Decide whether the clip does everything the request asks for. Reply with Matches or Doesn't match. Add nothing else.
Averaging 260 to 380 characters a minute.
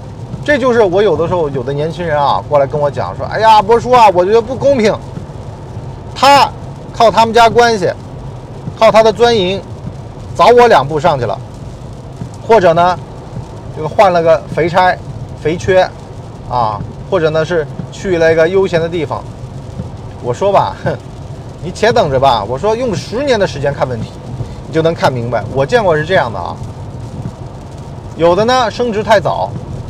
Doesn't match